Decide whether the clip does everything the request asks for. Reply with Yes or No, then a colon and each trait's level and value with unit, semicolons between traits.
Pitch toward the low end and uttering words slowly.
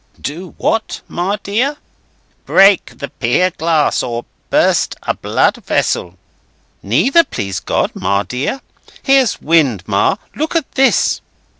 No: medium, 170 Hz; slow, 125 wpm